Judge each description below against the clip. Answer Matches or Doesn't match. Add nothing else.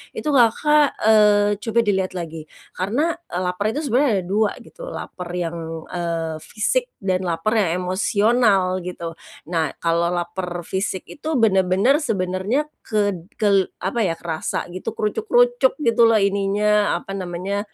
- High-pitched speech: Matches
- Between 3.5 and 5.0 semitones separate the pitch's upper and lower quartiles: Matches